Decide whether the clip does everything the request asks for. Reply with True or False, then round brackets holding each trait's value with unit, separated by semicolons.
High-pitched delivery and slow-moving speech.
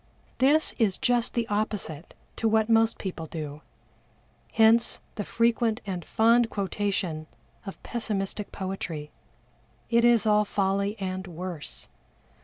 True (205 Hz; 120 wpm)